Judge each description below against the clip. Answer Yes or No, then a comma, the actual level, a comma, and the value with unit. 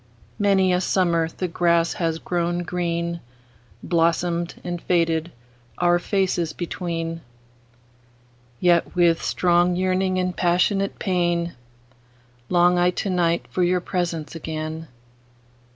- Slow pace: Yes, slow, 100 wpm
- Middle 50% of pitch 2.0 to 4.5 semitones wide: Yes, narrow, 2.5 semitones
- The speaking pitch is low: No, medium, 170 Hz